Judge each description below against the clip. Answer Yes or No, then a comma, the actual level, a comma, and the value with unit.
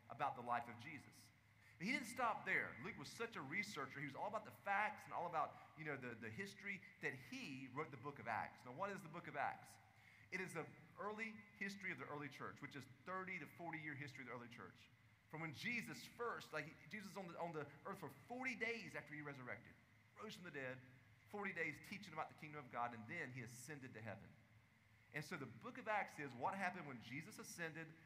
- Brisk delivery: Yes, fast, 235 wpm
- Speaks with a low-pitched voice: No, medium, 150 Hz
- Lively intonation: Yes, wide, 7.6 semitones